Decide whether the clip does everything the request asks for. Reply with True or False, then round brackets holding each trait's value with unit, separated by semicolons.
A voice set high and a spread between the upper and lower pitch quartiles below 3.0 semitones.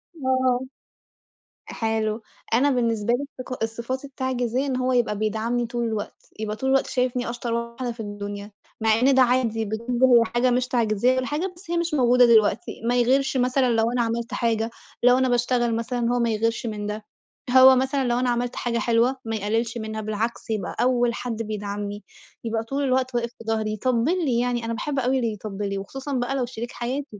True (240 Hz; 2.4 semitones)